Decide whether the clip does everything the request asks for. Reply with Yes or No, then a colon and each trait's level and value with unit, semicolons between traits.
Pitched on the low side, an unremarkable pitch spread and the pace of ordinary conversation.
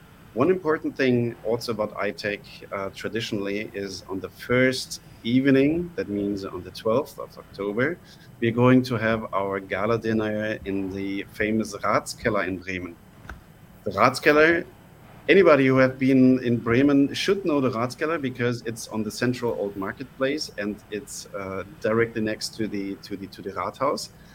Yes: low, 115 Hz; average, 4.4 semitones; average, 160 wpm